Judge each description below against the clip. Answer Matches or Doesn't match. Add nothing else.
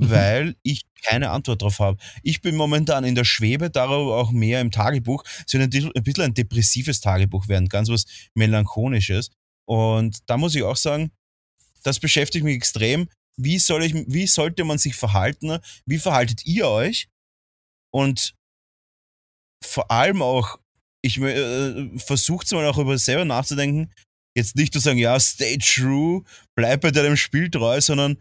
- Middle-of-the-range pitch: Doesn't match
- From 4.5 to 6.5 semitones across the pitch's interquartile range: Matches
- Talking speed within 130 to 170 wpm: Matches